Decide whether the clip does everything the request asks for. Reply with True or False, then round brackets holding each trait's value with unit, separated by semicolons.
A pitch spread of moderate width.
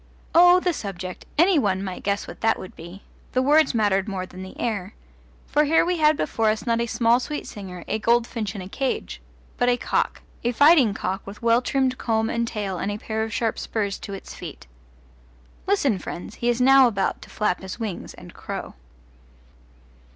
True (4.5 semitones)